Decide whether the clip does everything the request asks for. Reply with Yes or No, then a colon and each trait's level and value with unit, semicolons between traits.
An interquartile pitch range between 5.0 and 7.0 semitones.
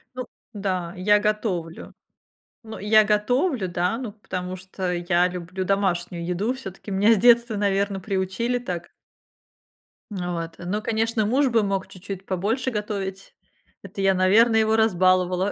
No: average, 3.1 semitones